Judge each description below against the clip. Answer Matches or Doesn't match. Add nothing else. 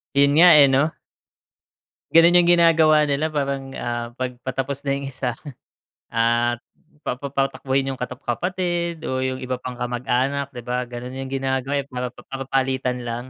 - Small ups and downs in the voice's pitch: Matches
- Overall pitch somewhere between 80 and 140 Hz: Matches